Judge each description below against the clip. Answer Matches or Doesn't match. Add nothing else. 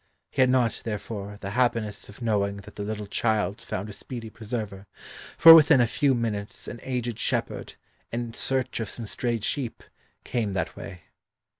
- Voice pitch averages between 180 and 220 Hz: Doesn't match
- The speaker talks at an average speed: Matches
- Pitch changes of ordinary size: Matches